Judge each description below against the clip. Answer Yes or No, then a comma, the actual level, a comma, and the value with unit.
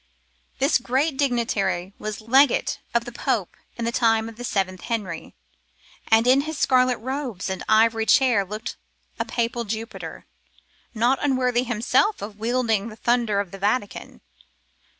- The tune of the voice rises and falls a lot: No, average, 3.0 semitones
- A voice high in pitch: Yes, high, 230 Hz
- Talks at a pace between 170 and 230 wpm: No, average, 150 wpm